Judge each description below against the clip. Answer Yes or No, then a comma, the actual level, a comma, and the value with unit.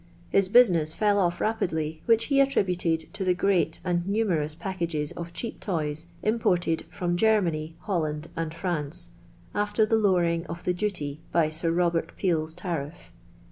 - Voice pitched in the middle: Yes, medium, 175 Hz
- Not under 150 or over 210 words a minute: Yes, average, 155 wpm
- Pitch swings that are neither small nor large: Yes, average, 3.7 semitones